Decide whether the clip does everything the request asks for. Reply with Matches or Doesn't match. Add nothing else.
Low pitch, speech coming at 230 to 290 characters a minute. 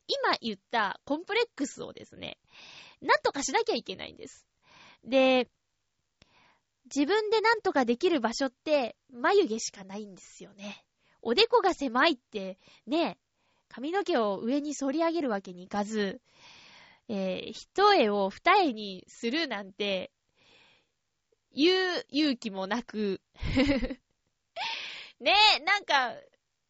Doesn't match